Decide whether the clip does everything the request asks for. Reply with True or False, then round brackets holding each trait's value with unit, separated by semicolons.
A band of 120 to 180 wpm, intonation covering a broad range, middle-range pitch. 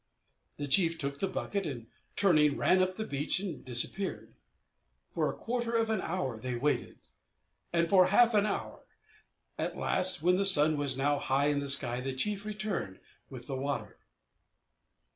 True (170 wpm; 6.1 semitones; 160 Hz)